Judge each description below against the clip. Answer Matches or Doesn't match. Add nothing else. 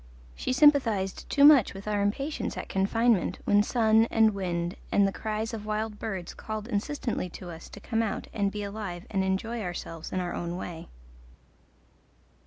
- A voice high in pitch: Matches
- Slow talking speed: Doesn't match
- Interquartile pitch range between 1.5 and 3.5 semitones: Matches